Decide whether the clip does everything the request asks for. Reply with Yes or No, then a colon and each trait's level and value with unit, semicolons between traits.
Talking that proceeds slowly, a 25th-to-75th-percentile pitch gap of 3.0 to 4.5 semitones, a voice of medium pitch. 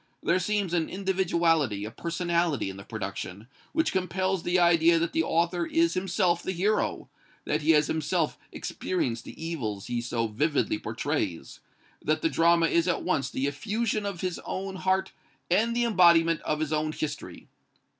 No: average, 165 wpm; average, 3.6 semitones; medium, 170 Hz